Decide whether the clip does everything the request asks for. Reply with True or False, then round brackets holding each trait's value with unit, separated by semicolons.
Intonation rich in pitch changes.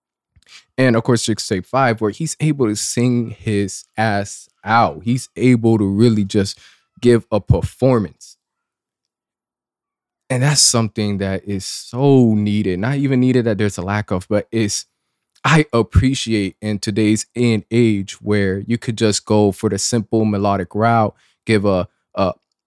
False (3.0 semitones)